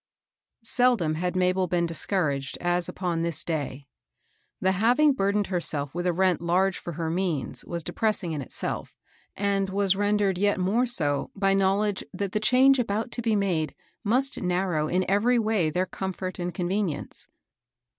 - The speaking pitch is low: No, medium, 185 Hz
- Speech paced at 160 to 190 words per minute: Yes, average, 165 wpm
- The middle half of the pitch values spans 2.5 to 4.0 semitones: Yes, average, 3.1 semitones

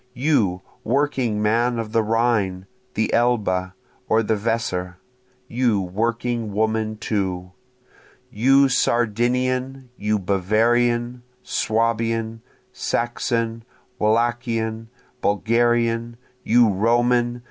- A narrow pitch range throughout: Yes, narrow, 2.0 semitones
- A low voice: Yes, low, 115 Hz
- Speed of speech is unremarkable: No, slow, 85 wpm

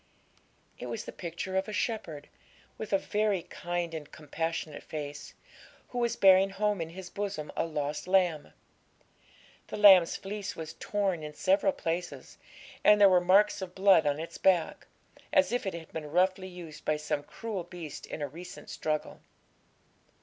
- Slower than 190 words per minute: Yes, average, 165 wpm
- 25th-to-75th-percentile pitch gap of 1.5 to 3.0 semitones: No, average, 3.7 semitones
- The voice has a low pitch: No, medium, 180 Hz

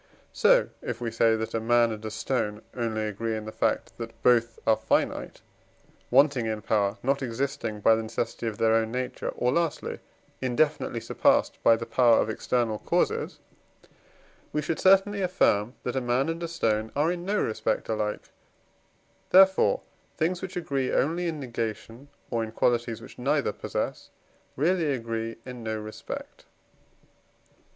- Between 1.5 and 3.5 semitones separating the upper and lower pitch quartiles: No, average, 4.4 semitones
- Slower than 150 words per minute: No, average, 160 wpm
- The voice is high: No, low, 120 Hz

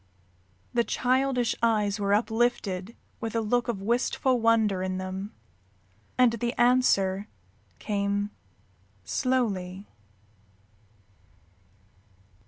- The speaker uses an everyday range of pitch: Yes, average, 3.4 semitones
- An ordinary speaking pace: No, slow, 85 wpm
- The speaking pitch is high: Yes, high, 220 Hz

